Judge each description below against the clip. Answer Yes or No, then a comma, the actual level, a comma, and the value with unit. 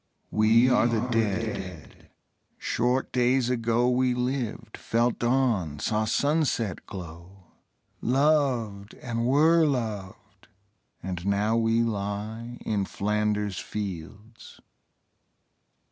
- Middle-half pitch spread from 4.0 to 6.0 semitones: No, average, 3.4 semitones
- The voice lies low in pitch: Yes, low, 115 Hz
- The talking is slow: Yes, slow, 95 wpm